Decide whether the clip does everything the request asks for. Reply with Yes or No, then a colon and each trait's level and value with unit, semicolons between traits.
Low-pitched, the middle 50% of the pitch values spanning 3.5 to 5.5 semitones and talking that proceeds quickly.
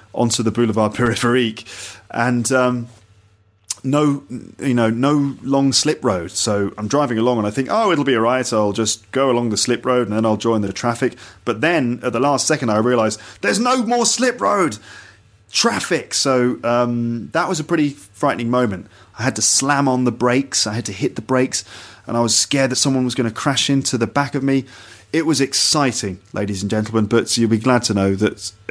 Yes: low, 120 Hz; average, 3.8 semitones; fast, 225 wpm